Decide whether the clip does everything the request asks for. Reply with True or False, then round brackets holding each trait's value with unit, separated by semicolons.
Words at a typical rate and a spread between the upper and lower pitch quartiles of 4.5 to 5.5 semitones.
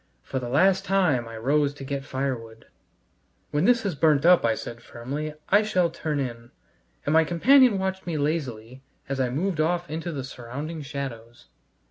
True (175 wpm; 5.1 semitones)